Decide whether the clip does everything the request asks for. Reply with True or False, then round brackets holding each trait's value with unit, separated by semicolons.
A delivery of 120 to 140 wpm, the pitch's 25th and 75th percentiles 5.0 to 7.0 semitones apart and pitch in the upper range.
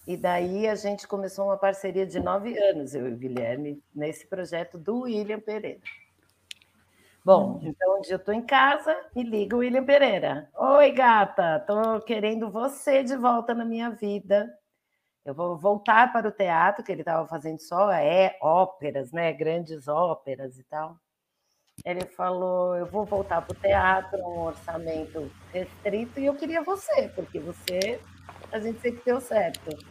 False (160 wpm; 5.5 semitones; 195 Hz)